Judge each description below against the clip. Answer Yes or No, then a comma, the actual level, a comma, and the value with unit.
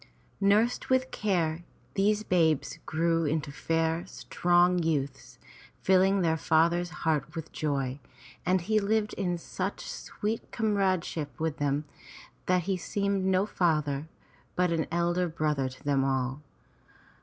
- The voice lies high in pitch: No, medium, 170 Hz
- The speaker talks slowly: Yes, slow, 130 wpm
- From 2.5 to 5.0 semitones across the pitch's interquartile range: Yes, average, 3.7 semitones